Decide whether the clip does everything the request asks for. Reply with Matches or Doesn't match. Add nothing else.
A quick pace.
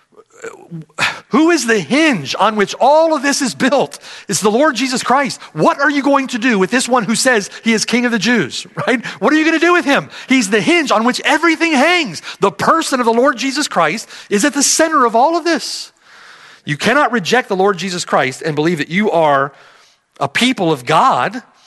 Matches